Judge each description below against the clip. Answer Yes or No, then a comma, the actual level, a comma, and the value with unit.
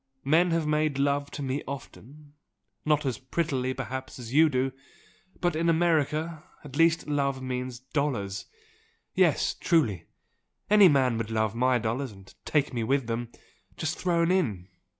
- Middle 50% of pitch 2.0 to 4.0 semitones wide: Yes, average, 3.7 semitones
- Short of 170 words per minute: Yes, average, 150 wpm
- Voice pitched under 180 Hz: Yes, medium, 140 Hz